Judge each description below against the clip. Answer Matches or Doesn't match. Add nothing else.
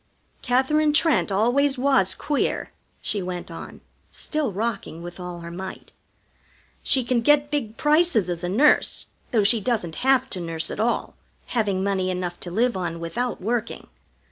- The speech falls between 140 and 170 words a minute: Matches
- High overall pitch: Matches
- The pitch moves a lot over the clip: Matches